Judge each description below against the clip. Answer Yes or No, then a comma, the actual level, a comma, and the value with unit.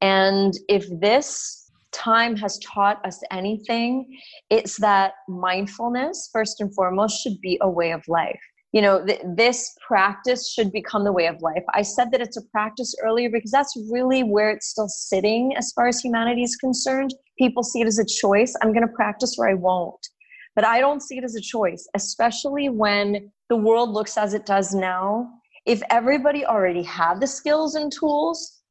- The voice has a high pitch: Yes, high, 225 Hz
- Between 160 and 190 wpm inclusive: Yes, average, 185 wpm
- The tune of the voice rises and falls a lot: No, average, 3.8 semitones